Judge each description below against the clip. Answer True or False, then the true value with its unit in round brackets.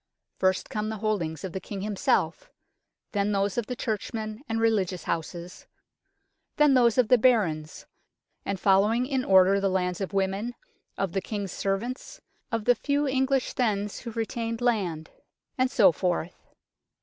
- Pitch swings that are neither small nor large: True (3.9 semitones)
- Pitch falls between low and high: False (210 Hz)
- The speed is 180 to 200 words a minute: False (155 wpm)